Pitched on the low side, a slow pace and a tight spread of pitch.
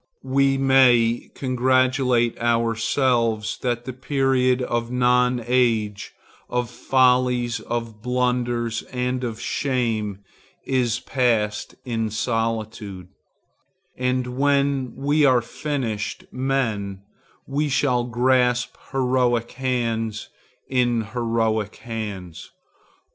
Yes: low, 125 Hz; slow, 90 wpm; narrow, 2.1 semitones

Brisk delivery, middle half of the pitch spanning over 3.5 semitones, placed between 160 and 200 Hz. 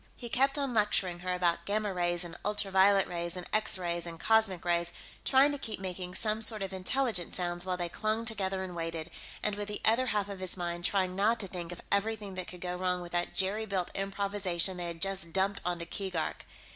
No: fast, 220 wpm; average, 2.9 semitones; high, 190 Hz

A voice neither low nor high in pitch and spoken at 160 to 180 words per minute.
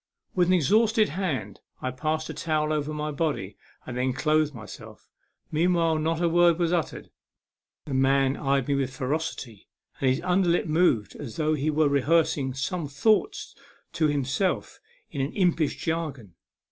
Yes: medium, 155 Hz; average, 165 wpm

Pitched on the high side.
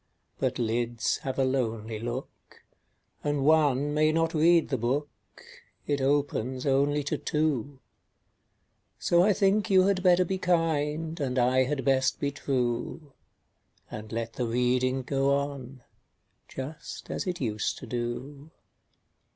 No: medium, 140 Hz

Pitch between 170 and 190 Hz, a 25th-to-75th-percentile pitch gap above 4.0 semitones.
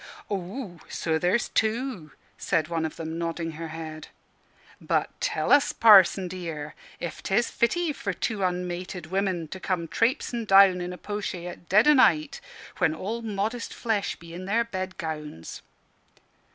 Yes: medium, 185 Hz; average, 4.6 semitones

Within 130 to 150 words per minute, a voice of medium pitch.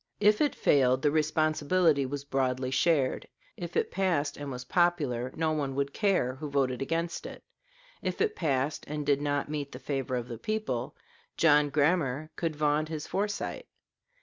No: average, 170 wpm; medium, 145 Hz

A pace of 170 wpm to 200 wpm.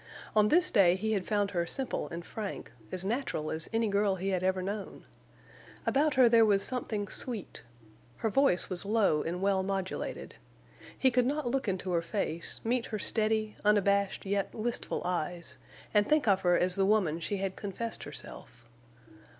Yes: average, 175 wpm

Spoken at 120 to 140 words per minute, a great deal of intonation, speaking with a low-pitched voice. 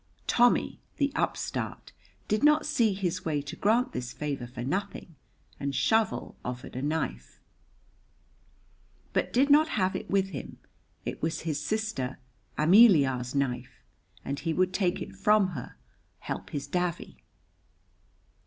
No: slow, 135 wpm; wide, 7.4 semitones; medium, 175 Hz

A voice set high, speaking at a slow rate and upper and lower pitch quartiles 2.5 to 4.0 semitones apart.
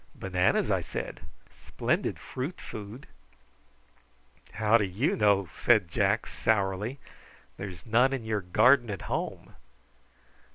No: low, 105 Hz; slow, 115 wpm; average, 3.5 semitones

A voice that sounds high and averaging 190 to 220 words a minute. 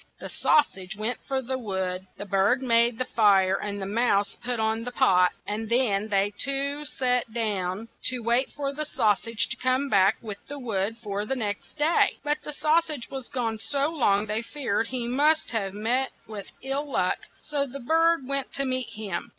Yes: high, 235 Hz; average, 195 wpm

